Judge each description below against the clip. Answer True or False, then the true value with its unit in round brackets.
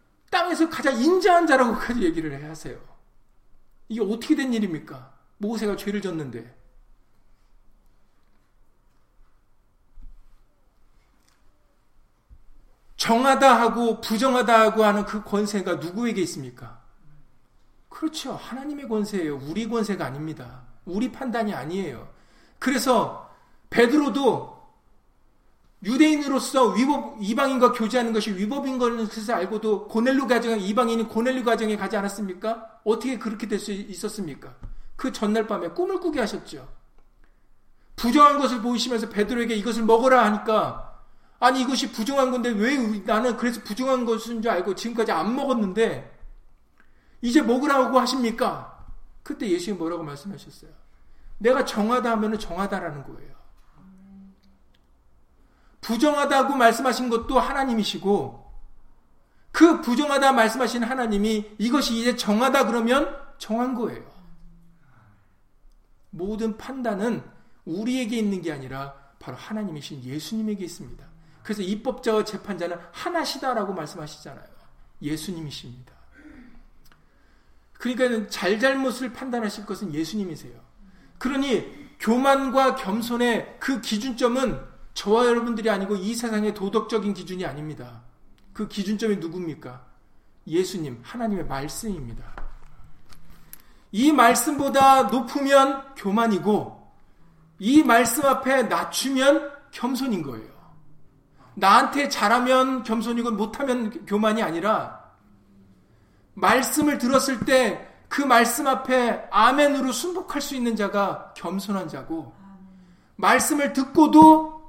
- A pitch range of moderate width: False (5.8 semitones)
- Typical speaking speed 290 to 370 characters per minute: False (280 characters per minute)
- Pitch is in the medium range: False (225 Hz)